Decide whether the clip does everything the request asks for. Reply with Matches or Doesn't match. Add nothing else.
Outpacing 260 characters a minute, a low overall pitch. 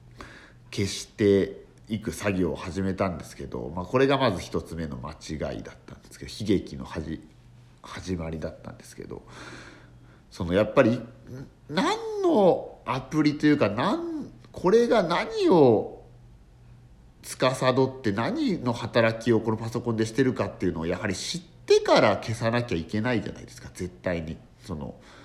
Matches